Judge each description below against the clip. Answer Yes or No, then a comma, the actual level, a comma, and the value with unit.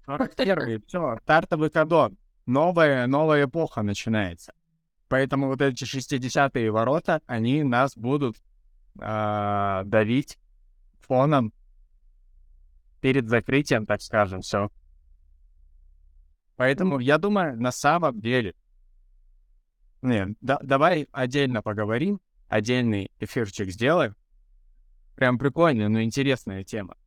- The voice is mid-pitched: No, low, 115 Hz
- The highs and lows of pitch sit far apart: Yes, wide, 6.4 semitones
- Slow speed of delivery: Yes, slow, 95 wpm